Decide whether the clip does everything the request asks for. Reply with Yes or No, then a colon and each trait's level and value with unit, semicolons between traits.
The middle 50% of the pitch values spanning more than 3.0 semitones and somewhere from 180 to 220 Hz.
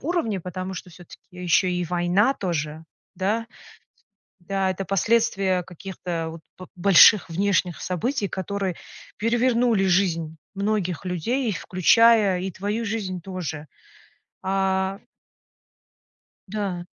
No: narrow, 2.6 semitones; high, 190 Hz